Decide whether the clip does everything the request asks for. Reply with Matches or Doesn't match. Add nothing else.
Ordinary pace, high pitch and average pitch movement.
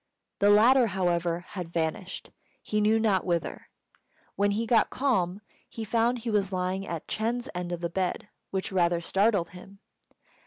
Matches